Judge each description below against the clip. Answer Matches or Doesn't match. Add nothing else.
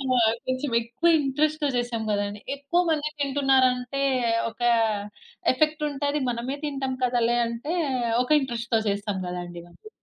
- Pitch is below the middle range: Doesn't match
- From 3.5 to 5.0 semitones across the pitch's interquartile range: Matches